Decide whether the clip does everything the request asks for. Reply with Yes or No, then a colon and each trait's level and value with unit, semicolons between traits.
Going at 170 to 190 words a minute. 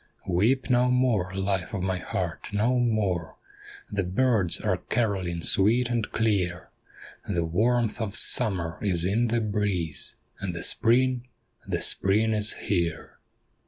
No: average, 140 wpm